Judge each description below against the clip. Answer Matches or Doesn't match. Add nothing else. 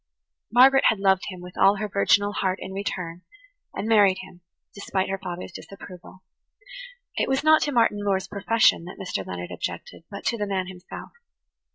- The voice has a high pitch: Matches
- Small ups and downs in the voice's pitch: Matches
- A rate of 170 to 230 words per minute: Matches